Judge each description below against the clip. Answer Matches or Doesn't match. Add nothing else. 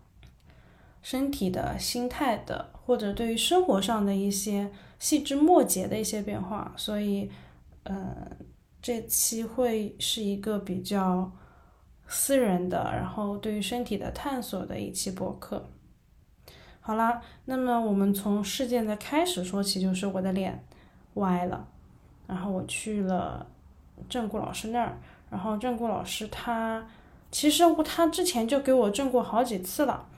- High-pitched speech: Matches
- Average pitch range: Matches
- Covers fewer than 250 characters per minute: Matches